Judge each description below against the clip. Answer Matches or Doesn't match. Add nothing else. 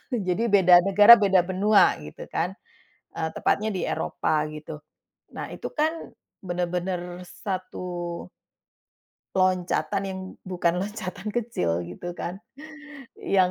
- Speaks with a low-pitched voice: Doesn't match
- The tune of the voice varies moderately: Doesn't match